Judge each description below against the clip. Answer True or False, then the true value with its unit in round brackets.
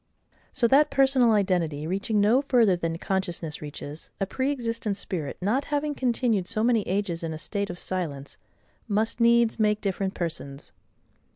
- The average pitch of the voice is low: False (205 Hz)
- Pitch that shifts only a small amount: False (5.3 semitones)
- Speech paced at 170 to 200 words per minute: False (160 wpm)